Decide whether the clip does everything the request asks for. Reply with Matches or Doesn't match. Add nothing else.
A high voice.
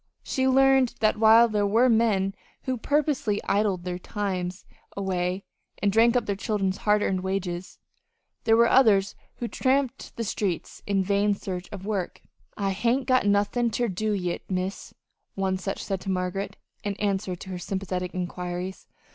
Matches